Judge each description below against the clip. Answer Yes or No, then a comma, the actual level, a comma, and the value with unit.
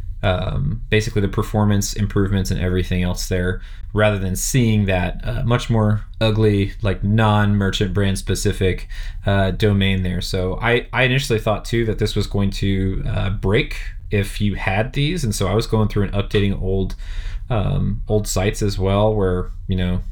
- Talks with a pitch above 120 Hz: No, low, 100 Hz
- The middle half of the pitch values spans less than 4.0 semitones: Yes, narrow, 2.4 semitones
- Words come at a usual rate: Yes, average, 175 wpm